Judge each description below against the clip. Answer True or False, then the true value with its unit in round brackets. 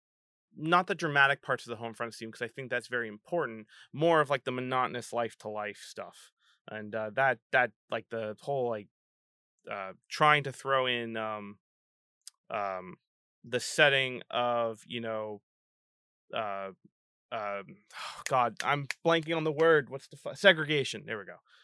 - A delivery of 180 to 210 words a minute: False (165 wpm)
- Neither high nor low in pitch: False (120 Hz)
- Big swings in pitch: False (4.7 semitones)